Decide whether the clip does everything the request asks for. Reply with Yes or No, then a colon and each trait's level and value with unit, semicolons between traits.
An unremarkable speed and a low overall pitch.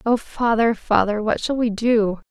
No: average, 180 wpm; high, 225 Hz